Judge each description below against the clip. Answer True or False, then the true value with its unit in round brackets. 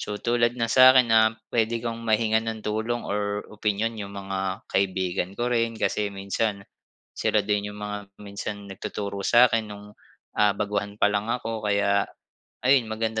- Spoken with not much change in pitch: True (2.1 semitones)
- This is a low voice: True (105 Hz)